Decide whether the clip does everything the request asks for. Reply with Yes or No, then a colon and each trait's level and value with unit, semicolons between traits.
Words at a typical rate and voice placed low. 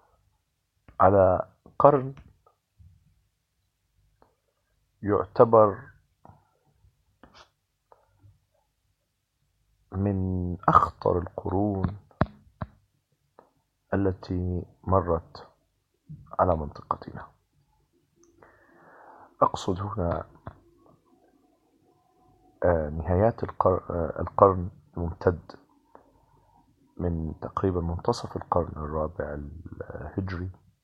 No: slow, 40 wpm; very low, 95 Hz